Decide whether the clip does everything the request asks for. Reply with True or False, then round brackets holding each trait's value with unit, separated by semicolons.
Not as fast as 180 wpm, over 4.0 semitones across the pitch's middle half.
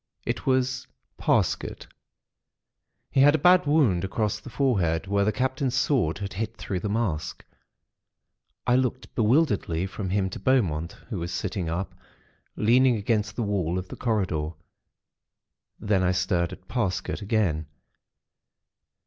True (140 wpm; 5.6 semitones)